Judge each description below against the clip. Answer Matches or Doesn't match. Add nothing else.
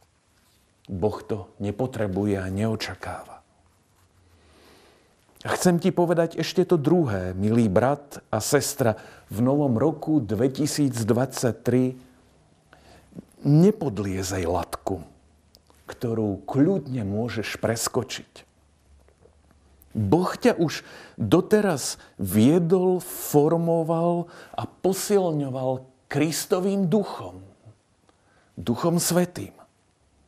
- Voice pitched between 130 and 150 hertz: Doesn't match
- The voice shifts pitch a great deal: Matches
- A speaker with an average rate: Doesn't match